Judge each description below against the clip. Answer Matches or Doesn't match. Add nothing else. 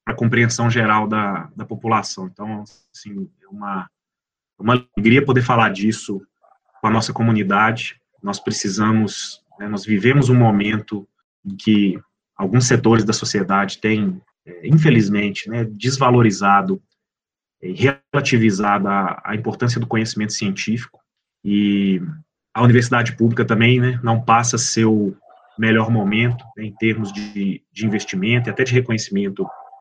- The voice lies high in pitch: Doesn't match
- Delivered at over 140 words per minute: Doesn't match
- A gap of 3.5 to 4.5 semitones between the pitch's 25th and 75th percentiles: Doesn't match